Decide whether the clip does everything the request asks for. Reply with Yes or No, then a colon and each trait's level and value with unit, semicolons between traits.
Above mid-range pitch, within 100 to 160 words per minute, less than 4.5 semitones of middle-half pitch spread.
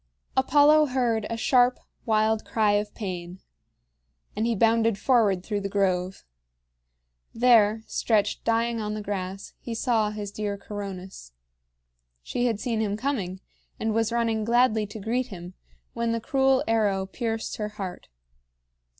Yes: high, 220 Hz; average, 140 wpm; narrow, 2.5 semitones